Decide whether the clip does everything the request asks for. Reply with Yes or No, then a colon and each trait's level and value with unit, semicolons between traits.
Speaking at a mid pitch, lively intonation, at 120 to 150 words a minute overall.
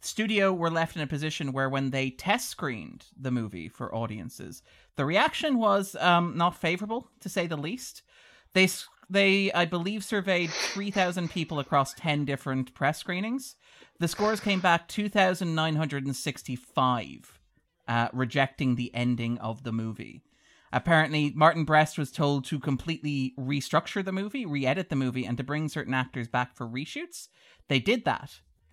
No: medium, 155 Hz; wide, 5.9 semitones; average, 165 wpm